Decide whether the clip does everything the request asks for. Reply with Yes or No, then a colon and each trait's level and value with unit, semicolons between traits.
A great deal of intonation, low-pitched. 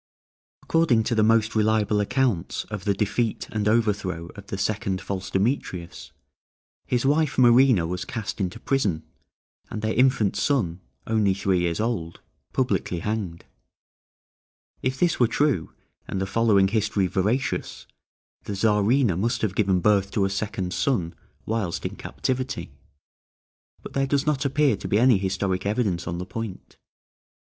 No: average, 4.0 semitones; low, 105 Hz